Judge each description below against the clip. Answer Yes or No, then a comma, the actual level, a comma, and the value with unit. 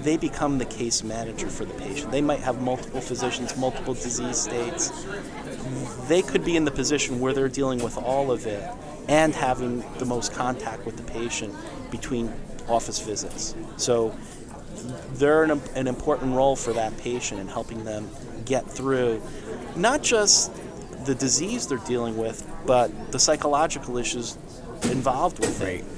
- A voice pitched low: Yes, low, 125 Hz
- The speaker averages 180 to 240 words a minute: No, average, 160 wpm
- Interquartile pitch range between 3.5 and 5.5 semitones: No, average, 2.9 semitones